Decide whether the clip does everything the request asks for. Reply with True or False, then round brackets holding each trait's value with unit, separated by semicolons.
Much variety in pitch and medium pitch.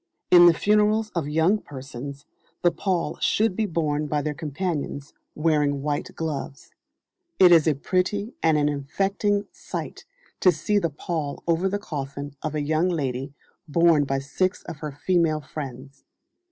False (4.1 semitones; 155 Hz)